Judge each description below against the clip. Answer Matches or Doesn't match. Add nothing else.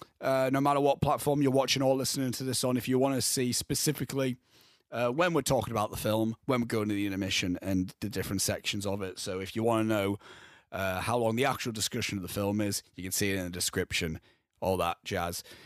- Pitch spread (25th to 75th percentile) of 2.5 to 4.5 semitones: Doesn't match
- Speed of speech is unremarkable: Doesn't match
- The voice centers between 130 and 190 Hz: Doesn't match